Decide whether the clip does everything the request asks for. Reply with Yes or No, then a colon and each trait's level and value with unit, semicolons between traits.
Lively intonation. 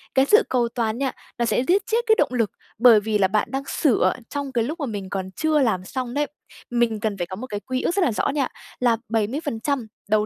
No: average, 4.6 semitones